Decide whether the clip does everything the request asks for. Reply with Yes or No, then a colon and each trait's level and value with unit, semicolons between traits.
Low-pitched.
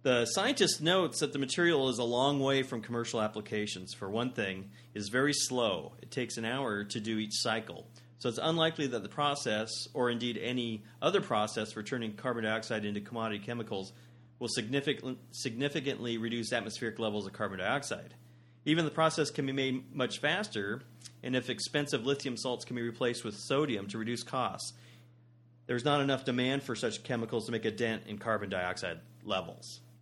Yes: low, 120 Hz